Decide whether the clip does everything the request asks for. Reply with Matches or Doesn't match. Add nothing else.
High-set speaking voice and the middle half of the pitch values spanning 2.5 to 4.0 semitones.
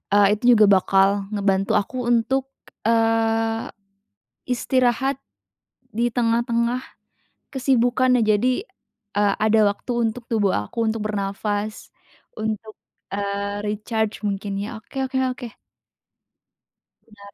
Matches